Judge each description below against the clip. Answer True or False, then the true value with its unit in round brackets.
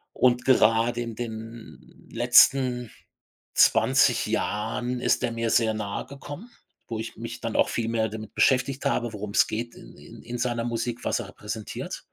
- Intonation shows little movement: True (1.8 semitones)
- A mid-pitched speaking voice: False (115 Hz)